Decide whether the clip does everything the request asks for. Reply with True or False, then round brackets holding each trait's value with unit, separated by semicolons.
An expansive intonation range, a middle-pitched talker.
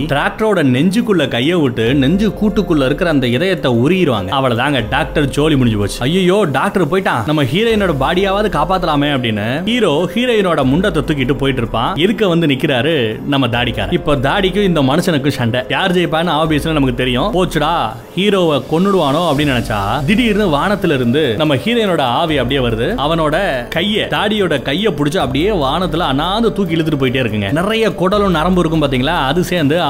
True (5.7 semitones; 155 Hz)